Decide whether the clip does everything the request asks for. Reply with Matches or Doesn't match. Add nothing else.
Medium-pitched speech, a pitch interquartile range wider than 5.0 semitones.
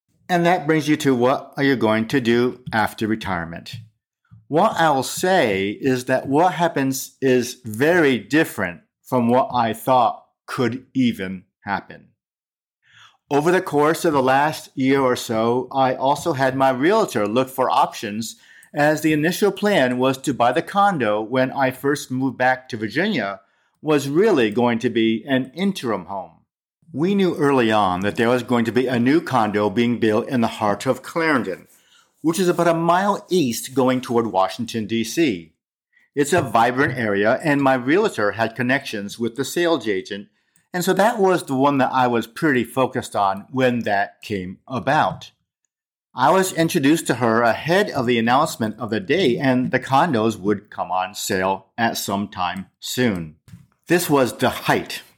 Doesn't match